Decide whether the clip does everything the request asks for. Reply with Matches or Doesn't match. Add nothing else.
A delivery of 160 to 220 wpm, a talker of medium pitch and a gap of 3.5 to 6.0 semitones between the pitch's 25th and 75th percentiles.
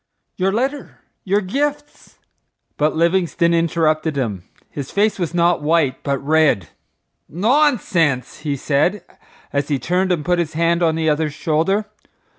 Doesn't match